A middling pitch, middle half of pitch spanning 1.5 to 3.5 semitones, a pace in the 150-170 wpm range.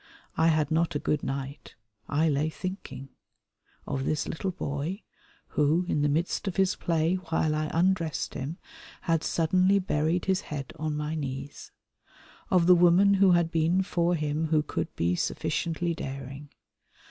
Yes: medium, 160 Hz; average, 3.0 semitones; average, 160 wpm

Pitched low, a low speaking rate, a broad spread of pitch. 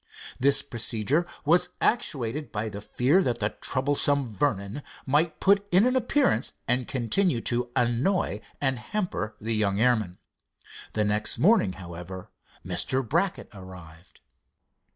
Yes: low, 125 Hz; slow, 130 wpm; wide, 6.4 semitones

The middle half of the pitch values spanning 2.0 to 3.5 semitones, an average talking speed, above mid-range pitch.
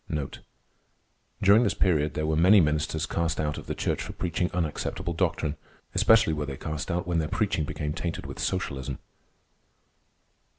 No: average, 2.8 semitones; average, 160 wpm; very low, 80 Hz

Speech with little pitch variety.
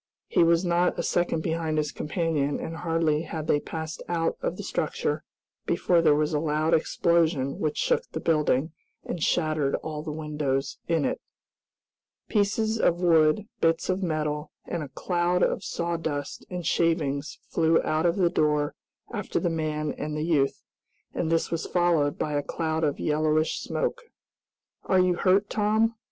Yes: narrow, 2.3 semitones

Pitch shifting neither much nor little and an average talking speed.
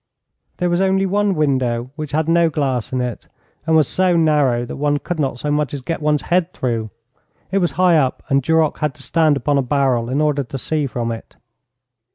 No: average, 3.9 semitones; fast, 215 wpm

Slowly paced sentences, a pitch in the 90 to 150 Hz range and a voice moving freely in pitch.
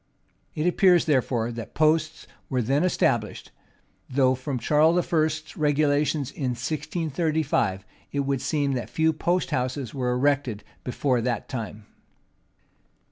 No: slow, 125 wpm; medium, 140 Hz; average, 3.8 semitones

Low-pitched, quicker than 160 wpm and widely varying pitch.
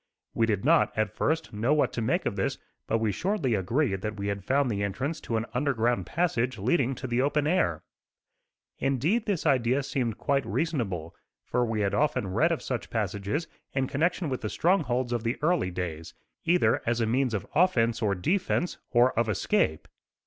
Yes: low, 120 Hz; average, 190 wpm; wide, 5.7 semitones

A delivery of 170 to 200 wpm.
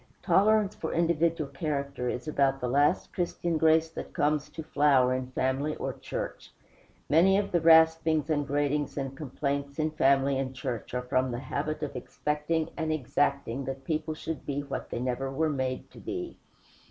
Yes: average, 175 wpm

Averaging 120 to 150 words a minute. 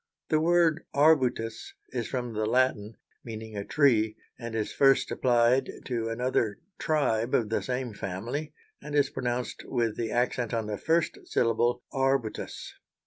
Yes: average, 145 wpm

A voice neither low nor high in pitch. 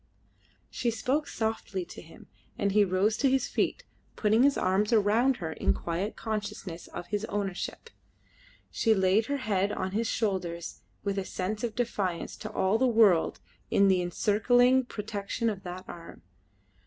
No: high, 205 Hz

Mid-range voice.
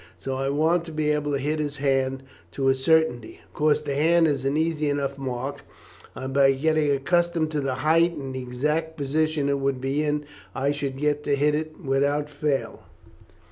Yes: medium, 145 Hz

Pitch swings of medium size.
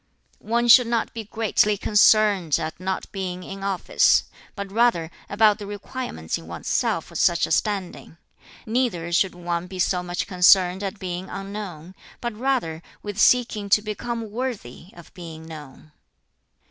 Yes: average, 3.6 semitones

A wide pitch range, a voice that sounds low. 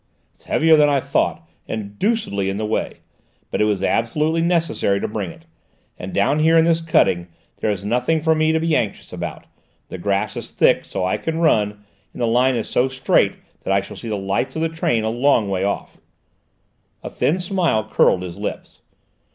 Yes: wide, 8.0 semitones; low, 120 Hz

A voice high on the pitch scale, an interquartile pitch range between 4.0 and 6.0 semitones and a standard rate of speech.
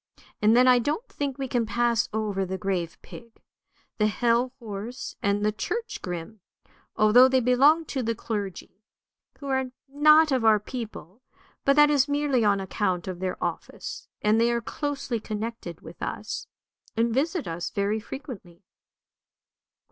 Yes: high, 230 Hz; average, 4.5 semitones; average, 160 wpm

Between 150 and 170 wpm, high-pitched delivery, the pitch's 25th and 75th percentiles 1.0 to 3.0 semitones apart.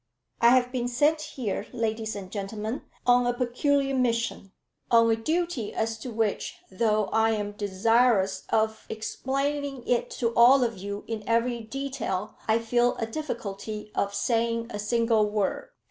Yes: average, 155 wpm; high, 230 Hz; narrow, 2.5 semitones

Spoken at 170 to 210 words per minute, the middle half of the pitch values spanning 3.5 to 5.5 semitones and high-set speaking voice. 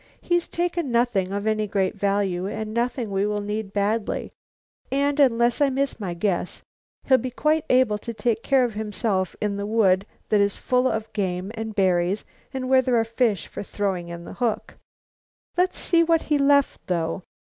Yes: average, 185 wpm; average, 4.3 semitones; high, 220 Hz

